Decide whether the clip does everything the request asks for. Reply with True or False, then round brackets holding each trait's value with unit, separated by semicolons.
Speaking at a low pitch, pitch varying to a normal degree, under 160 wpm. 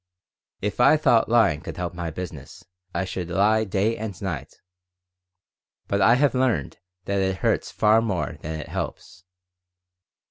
True (95 Hz; 4.2 semitones; 150 wpm)